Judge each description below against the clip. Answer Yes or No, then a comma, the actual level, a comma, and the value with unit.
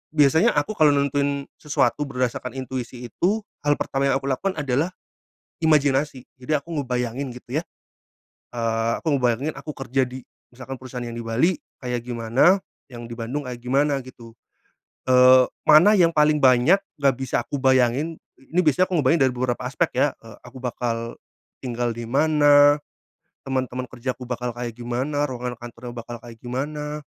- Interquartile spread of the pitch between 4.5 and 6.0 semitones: No, average, 3.1 semitones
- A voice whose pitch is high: No, low, 130 Hz